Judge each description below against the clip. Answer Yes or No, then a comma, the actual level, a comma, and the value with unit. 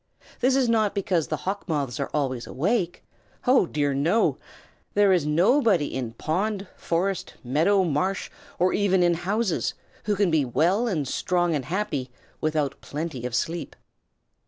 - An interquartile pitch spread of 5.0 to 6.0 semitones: Yes, wide, 5.5 semitones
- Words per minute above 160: No, average, 155 wpm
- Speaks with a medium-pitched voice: Yes, medium, 175 Hz